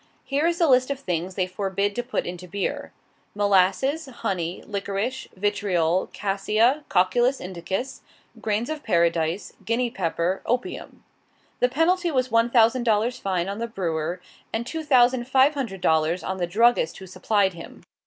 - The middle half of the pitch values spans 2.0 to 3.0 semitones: No, wide, 5.4 semitones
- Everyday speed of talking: Yes, average, 155 wpm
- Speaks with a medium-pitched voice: No, high, 205 Hz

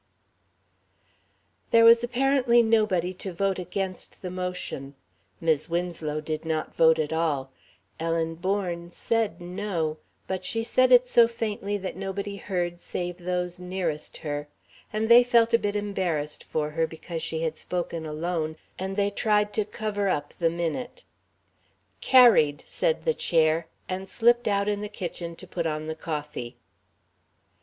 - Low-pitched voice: No, medium, 180 Hz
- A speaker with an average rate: Yes, average, 150 wpm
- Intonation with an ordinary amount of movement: Yes, average, 4.3 semitones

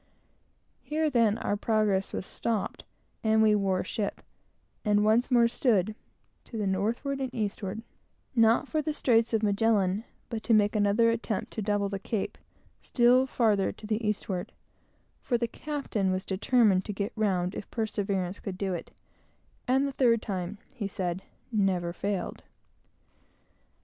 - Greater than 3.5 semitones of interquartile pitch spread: No, average, 2.9 semitones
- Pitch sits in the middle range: No, high, 215 Hz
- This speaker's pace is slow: No, average, 150 wpm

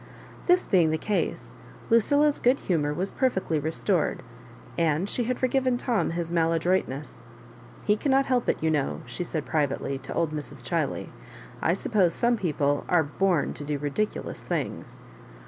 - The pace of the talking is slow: No, average, 165 wpm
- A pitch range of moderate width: No, wide, 7.2 semitones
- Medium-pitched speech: Yes, medium, 175 Hz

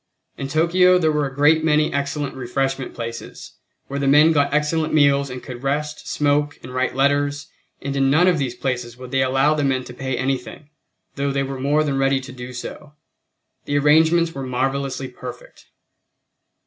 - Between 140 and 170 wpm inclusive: No, average, 185 wpm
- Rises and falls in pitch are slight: Yes, narrow, 2.2 semitones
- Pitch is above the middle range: No, medium, 140 Hz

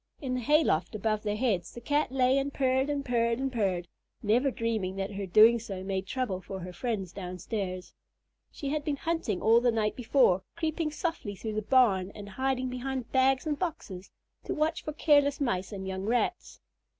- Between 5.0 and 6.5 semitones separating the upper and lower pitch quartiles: Yes, wide, 5.6 semitones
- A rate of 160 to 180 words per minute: No, average, 195 wpm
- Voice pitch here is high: Yes, high, 235 Hz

